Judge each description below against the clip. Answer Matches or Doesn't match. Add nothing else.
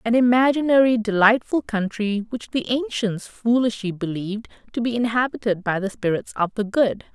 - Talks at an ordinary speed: Matches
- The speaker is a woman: Matches